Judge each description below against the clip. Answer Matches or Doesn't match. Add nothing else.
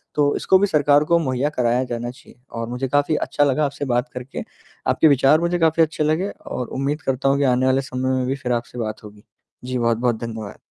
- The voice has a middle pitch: Doesn't match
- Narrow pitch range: Doesn't match